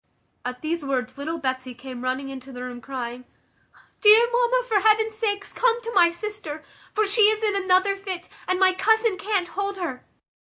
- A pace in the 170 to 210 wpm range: Yes, average, 185 wpm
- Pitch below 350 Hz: No, very high, 370 Hz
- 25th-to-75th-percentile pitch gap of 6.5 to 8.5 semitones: Yes, wide, 8.0 semitones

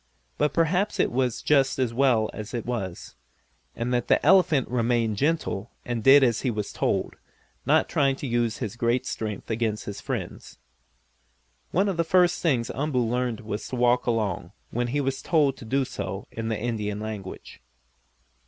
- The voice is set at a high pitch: No, low, 120 Hz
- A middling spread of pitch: Yes, average, 3.7 semitones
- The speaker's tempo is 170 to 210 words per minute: Yes, average, 175 wpm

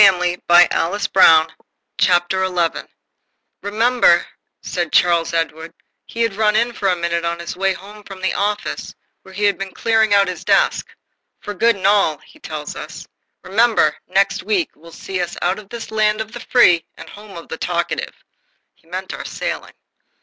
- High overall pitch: Yes, high, 195 Hz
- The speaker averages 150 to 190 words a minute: Yes, average, 175 wpm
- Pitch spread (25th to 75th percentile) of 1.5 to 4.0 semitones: Yes, average, 3.7 semitones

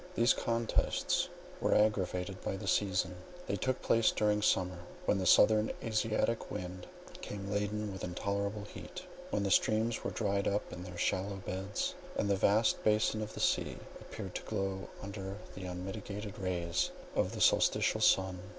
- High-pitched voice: No, low, 100 Hz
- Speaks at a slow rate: No, average, 160 wpm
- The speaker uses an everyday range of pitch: No, narrow, 2.2 semitones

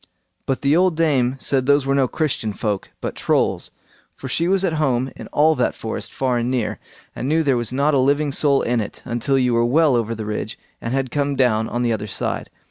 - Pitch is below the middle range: Yes, low, 130 Hz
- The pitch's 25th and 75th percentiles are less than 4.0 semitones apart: Yes, average, 3.3 semitones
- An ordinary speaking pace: No, fast, 230 wpm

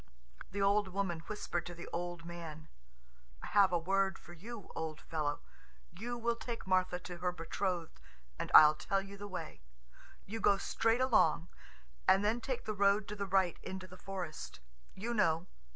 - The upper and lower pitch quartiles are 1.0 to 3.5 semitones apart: Yes, average, 2.9 semitones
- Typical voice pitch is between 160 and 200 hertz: Yes, high, 190 Hz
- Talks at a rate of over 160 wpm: Yes, average, 175 wpm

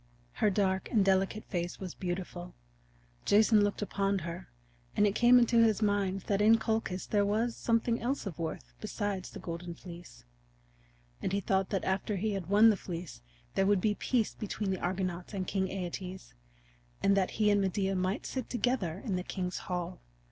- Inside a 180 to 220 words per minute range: Yes, average, 185 wpm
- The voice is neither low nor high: No, high, 195 Hz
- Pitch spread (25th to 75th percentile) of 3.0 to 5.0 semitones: No, narrow, 2.5 semitones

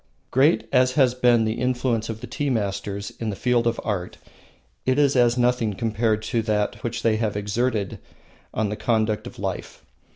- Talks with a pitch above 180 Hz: No, low, 115 Hz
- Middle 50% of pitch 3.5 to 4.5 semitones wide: No, narrow, 2.5 semitones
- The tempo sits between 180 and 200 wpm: Yes, average, 185 wpm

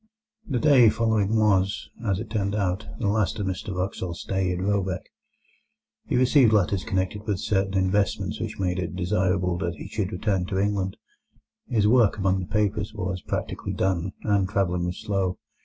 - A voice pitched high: No, very low, 95 Hz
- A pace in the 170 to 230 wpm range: Yes, average, 175 wpm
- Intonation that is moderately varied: No, narrow, 2.3 semitones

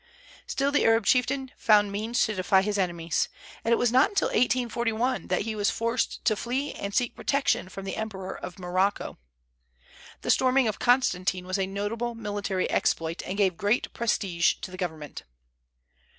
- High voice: Yes, high, 210 Hz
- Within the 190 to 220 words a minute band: No, average, 170 wpm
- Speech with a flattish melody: No, average, 4.1 semitones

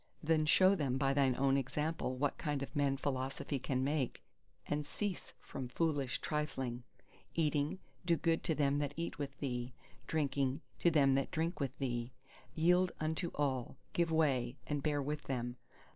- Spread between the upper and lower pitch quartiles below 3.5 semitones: Yes, average, 2.8 semitones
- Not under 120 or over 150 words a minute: No, average, 165 wpm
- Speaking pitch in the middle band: Yes, medium, 145 Hz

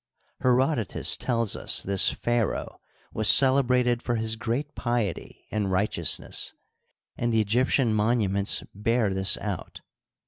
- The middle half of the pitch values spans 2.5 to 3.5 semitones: Yes, average, 2.8 semitones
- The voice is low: Yes, low, 115 Hz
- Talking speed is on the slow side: Yes, slow, 125 wpm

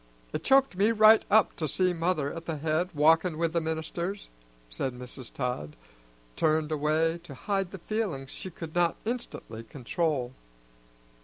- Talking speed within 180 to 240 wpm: No, average, 155 wpm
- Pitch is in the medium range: Yes, medium, 165 Hz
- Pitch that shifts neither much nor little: Yes, average, 3.9 semitones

